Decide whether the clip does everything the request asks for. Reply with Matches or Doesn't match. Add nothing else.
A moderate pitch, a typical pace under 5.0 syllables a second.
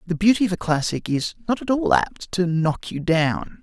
Matches